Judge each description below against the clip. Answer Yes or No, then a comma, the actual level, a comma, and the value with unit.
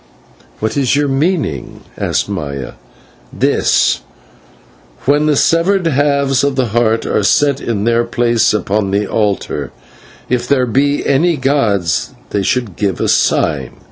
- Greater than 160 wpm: No, average, 140 wpm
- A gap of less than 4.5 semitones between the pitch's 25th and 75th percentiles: No, wide, 5.4 semitones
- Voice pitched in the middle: No, low, 125 Hz